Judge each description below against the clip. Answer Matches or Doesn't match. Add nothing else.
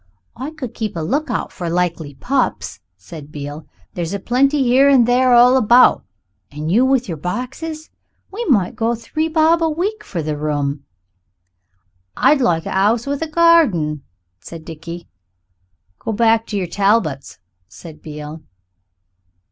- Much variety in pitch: Matches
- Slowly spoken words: Doesn't match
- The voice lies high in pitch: Matches